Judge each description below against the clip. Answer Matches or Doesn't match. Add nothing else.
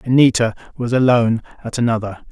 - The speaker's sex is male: Matches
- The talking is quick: Doesn't match